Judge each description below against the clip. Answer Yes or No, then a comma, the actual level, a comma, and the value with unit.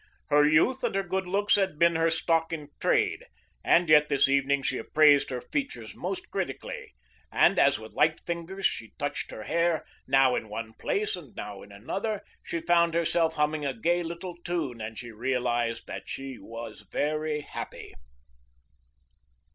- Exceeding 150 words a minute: Yes, average, 170 wpm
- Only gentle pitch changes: No, average, 5.1 semitones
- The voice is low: No, medium, 155 Hz